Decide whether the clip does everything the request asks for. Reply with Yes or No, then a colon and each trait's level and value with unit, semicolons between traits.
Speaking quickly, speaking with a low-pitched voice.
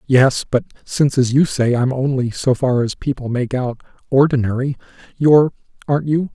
No: average, 160 wpm; low, 130 Hz